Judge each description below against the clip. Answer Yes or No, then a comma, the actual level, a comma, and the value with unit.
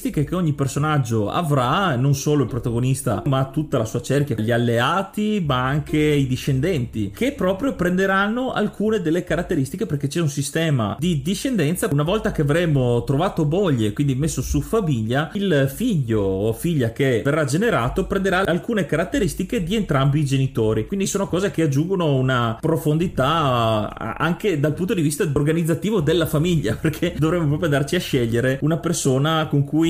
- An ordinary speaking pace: Yes, average, 160 wpm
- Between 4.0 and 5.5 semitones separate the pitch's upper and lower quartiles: Yes, average, 4.8 semitones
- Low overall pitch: No, medium, 150 Hz